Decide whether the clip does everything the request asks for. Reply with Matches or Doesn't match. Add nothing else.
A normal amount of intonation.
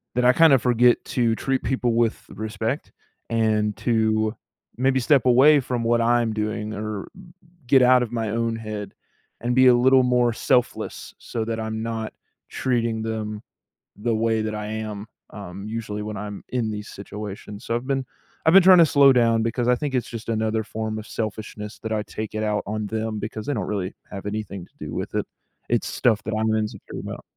Doesn't match